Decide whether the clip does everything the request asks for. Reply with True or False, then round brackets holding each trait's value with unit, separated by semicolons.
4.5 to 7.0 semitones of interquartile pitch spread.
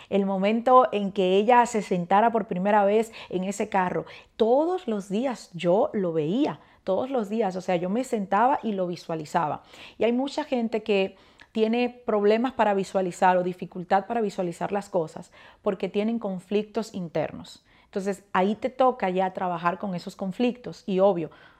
False (3.3 semitones)